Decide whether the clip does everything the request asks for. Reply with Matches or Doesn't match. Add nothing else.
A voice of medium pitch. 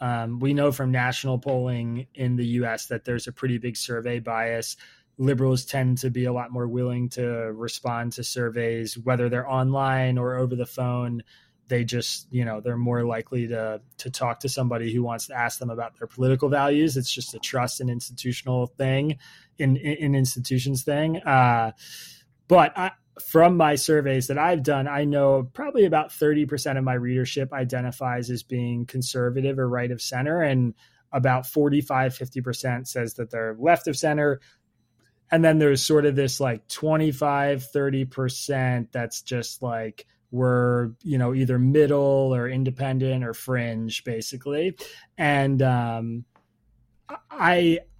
Doesn't match